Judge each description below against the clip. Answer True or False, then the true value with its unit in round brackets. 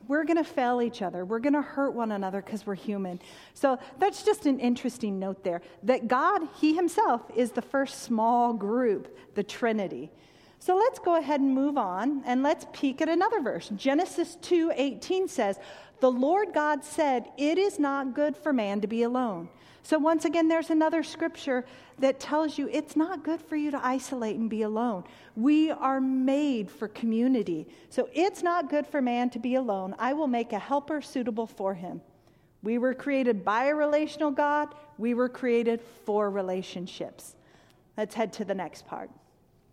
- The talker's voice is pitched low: False (260 Hz)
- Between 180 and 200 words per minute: True (185 wpm)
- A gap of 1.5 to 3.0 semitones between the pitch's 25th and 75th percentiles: False (5.2 semitones)